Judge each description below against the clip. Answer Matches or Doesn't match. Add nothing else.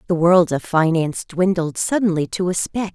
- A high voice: Doesn't match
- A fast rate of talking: Doesn't match